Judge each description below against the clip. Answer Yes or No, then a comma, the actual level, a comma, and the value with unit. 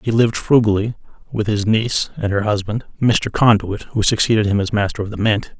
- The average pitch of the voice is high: No, low, 105 Hz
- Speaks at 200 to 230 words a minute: Yes, fast, 205 wpm